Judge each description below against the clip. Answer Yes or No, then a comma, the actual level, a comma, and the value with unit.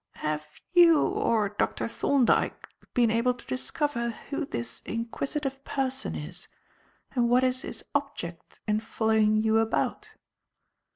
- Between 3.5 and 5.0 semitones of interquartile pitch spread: Yes, average, 4.1 semitones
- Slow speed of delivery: Yes, slow, 125 wpm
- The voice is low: No, high, 235 Hz